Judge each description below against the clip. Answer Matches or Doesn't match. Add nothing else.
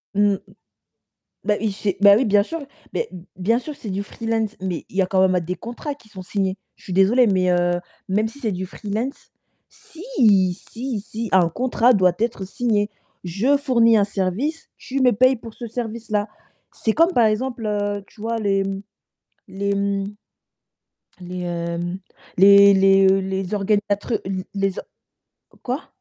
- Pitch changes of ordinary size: Matches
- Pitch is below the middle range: Doesn't match